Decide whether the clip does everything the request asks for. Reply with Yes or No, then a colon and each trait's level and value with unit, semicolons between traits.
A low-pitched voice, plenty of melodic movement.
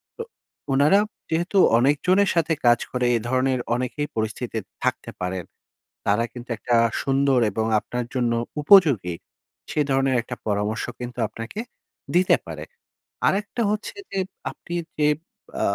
Yes: low, 130 Hz; wide, 5.7 semitones